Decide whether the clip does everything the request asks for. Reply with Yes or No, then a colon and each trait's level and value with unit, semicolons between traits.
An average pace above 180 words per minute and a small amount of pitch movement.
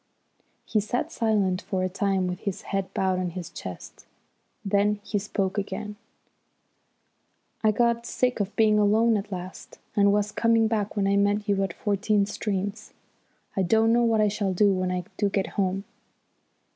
No: average, 170 wpm; narrow, 1.9 semitones